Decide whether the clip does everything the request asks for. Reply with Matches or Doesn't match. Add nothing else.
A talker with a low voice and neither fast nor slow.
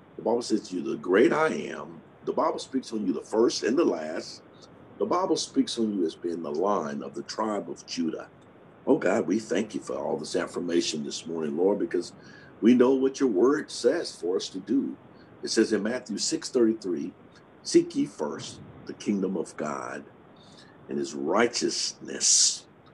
Matches